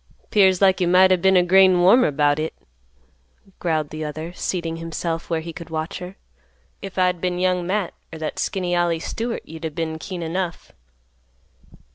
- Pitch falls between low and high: Yes, medium, 175 Hz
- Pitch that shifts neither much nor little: No, narrow, 2.3 semitones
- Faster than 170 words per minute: Yes, average, 180 wpm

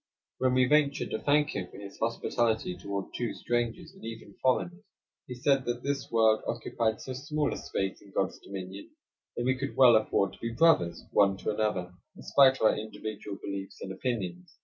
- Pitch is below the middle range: Yes, low, 115 Hz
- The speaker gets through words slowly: No, average, 200 wpm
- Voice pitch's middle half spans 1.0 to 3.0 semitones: No, average, 4.7 semitones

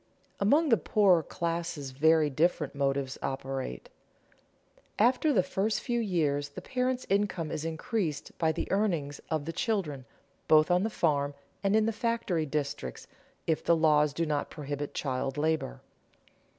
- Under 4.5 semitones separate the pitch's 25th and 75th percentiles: No, wide, 5.6 semitones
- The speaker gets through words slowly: No, average, 150 wpm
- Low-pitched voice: No, medium, 160 Hz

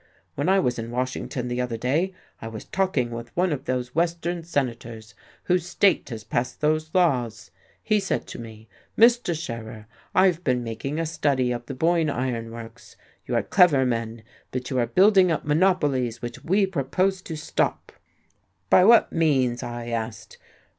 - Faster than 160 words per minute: Yes, average, 170 wpm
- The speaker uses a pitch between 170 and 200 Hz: No, low, 130 Hz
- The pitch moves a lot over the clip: Yes, wide, 6.5 semitones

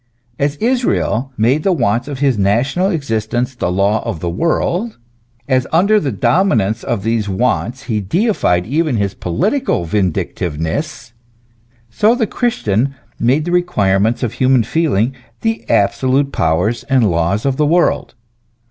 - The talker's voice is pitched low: Yes, low, 125 Hz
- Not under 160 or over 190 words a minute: No, average, 140 wpm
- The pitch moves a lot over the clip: Yes, wide, 7.1 semitones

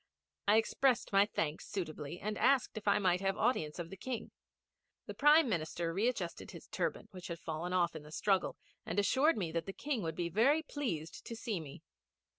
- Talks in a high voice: Yes, high, 195 Hz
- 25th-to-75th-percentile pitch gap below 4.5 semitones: No, wide, 5.5 semitones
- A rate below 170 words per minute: No, average, 200 wpm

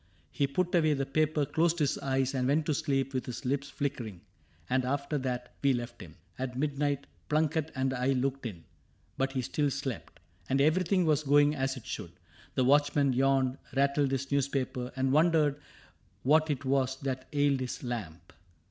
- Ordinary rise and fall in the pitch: No, narrow, 2.1 semitones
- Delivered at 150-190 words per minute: Yes, average, 180 wpm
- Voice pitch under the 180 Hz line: Yes, low, 135 Hz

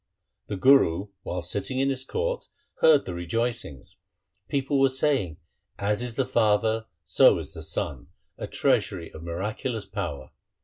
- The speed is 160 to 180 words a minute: No, average, 150 wpm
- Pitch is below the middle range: Yes, low, 110 Hz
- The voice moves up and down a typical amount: No, wide, 6.8 semitones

